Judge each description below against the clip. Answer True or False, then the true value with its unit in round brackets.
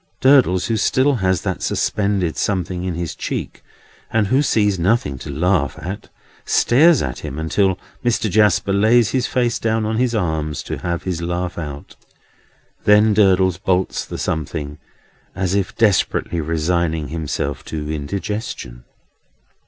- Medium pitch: False (95 Hz)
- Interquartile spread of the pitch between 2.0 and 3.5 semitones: False (4.8 semitones)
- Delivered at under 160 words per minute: True (145 wpm)